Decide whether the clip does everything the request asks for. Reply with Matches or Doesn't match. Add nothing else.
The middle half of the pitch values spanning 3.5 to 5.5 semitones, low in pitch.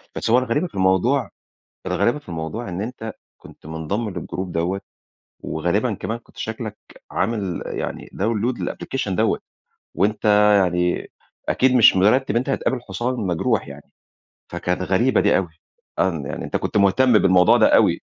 Matches